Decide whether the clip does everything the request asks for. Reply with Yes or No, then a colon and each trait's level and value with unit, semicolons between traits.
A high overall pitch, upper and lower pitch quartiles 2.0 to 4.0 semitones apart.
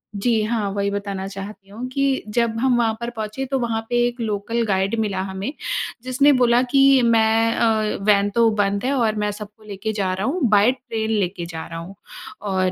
Yes: high, 220 Hz; average, 3.0 semitones